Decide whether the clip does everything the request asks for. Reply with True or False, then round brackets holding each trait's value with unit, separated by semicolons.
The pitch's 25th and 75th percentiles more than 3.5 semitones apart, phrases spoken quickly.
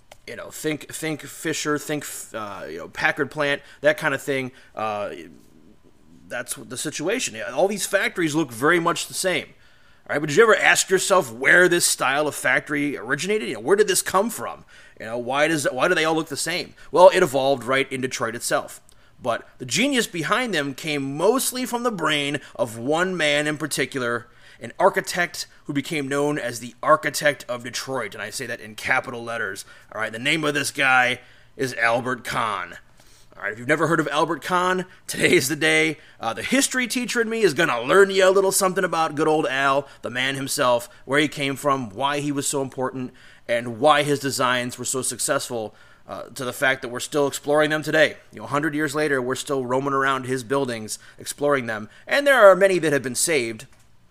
True (4.6 semitones; 210 wpm)